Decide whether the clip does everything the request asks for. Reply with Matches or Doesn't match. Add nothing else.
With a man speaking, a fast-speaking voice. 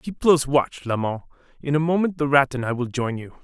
Matches